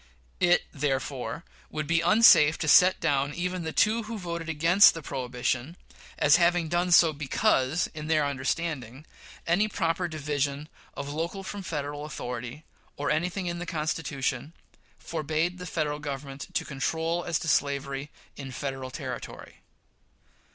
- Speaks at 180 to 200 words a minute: No, average, 145 wpm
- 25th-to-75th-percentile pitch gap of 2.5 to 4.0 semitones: Yes, average, 3.5 semitones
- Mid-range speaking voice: Yes, medium, 155 Hz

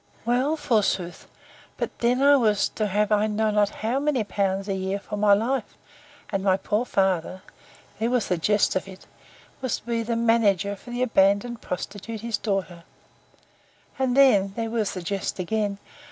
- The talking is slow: No, average, 175 wpm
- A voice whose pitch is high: Yes, high, 210 Hz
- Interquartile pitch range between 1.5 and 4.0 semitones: Yes, average, 3.1 semitones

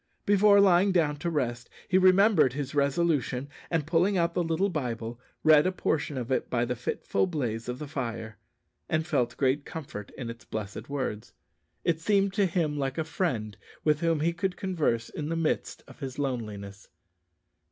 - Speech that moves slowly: No, average, 180 wpm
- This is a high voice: No, medium, 150 Hz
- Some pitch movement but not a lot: No, wide, 5.7 semitones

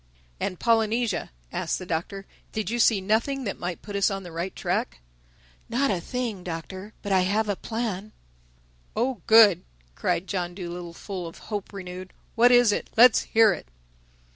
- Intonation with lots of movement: No, average, 3.7 semitones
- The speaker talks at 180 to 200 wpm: No, average, 165 wpm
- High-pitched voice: Yes, high, 200 Hz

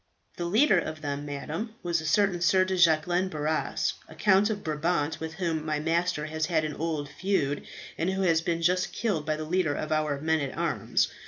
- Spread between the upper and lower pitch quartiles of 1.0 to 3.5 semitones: Yes, average, 2.9 semitones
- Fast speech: Yes, fast, 210 wpm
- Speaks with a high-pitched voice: No, medium, 160 Hz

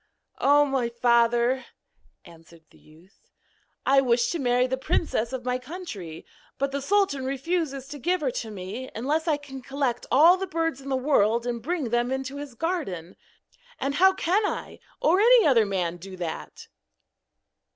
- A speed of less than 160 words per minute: No, average, 170 wpm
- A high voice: Yes, very high, 265 Hz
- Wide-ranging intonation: No, average, 4.5 semitones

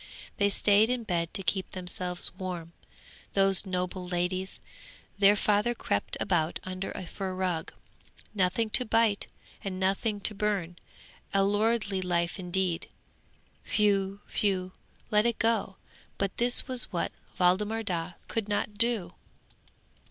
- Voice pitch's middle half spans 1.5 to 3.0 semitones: Yes, narrow, 2.6 semitones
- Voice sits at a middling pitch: No, high, 195 Hz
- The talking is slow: Yes, slow, 130 wpm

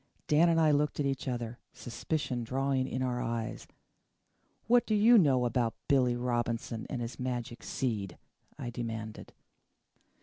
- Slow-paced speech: No, average, 145 wpm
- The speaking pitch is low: Yes, low, 125 Hz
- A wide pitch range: No, average, 3.0 semitones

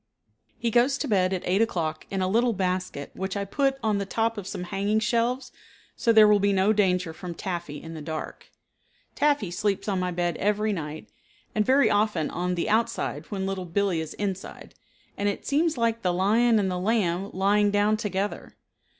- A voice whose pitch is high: Yes, high, 200 Hz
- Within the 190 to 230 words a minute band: Yes, average, 195 wpm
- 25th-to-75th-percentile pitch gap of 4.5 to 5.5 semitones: No, average, 3.3 semitones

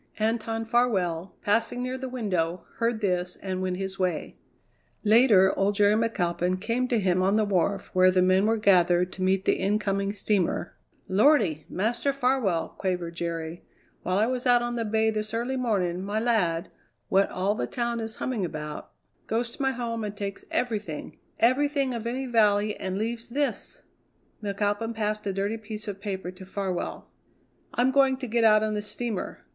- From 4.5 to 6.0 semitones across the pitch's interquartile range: No, average, 3.9 semitones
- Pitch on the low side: No, high, 210 Hz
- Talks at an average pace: Yes, average, 180 wpm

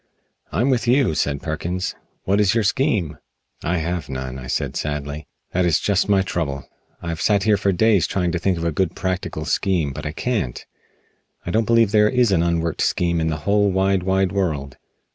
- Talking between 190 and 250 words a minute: Yes, average, 200 wpm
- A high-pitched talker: No, very low, 90 Hz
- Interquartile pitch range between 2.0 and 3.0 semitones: No, average, 4.3 semitones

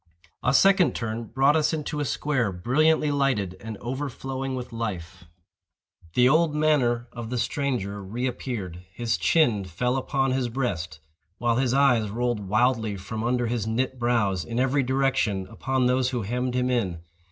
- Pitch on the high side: No, low, 125 Hz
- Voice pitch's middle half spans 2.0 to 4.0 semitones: Yes, average, 3.5 semitones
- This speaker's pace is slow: No, average, 165 wpm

